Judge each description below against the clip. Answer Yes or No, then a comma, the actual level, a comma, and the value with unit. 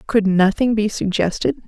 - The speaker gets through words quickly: No, average, 145 wpm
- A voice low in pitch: No, high, 205 Hz